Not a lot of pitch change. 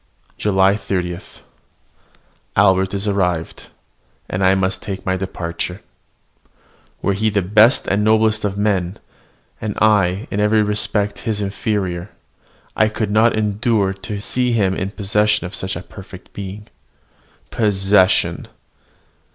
Yes: narrow, 2.0 semitones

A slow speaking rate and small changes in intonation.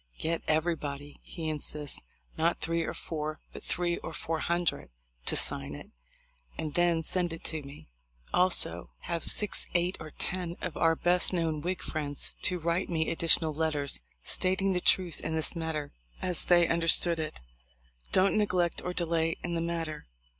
No: average, 165 wpm; narrow, 1.9 semitones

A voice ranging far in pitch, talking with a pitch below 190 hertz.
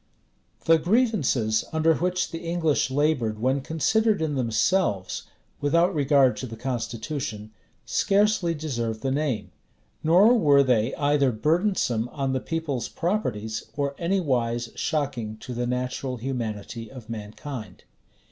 Yes: wide, 5.7 semitones; low, 135 Hz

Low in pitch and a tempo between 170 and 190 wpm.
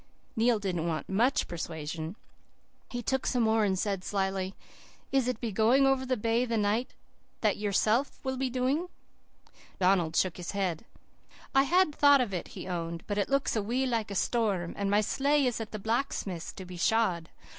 No: high, 215 Hz; average, 185 wpm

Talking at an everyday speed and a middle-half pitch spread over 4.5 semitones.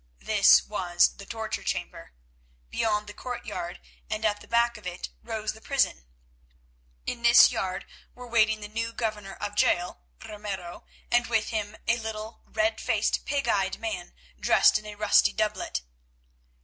No: average, 160 wpm; narrow, 2.4 semitones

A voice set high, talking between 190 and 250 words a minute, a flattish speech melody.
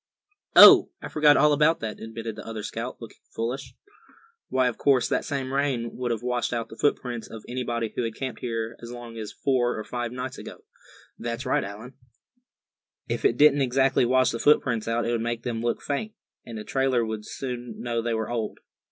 No: low, 120 Hz; fast, 205 wpm; narrow, 2.3 semitones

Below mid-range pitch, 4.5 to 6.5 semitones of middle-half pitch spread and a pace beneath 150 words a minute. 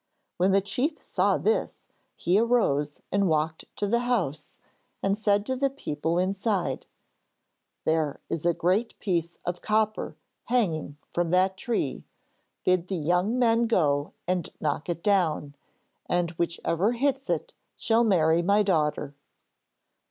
No: medium, 185 Hz; average, 5.2 semitones; slow, 135 wpm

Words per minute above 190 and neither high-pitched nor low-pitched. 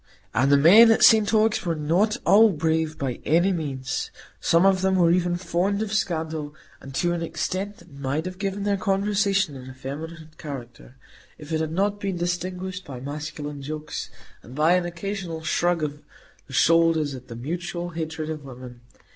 No: average, 180 wpm; medium, 165 Hz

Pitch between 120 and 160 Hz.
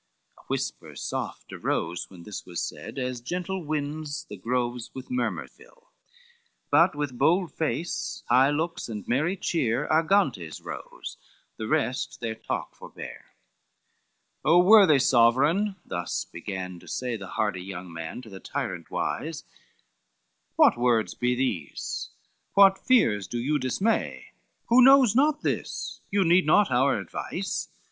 Yes: low, 135 Hz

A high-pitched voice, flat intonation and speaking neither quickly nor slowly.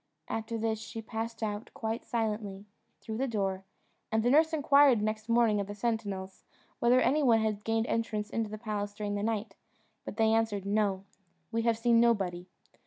Yes: high, 220 Hz; narrow, 1.9 semitones; average, 180 wpm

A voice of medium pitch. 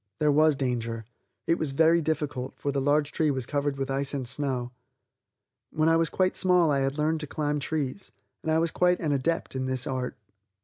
Yes: medium, 145 Hz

